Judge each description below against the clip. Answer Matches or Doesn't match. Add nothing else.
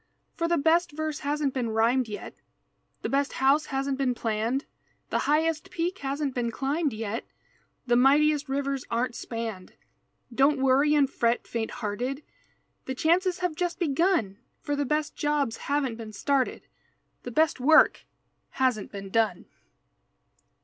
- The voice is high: Matches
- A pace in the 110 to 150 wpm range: Matches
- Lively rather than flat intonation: Doesn't match